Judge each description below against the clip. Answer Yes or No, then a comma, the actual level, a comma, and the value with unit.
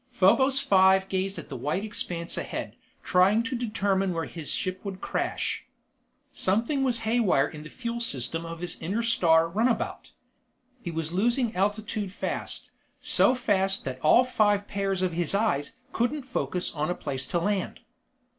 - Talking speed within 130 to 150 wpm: No, average, 160 wpm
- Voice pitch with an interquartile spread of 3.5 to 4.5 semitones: No, average, 5.1 semitones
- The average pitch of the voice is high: Yes, high, 195 Hz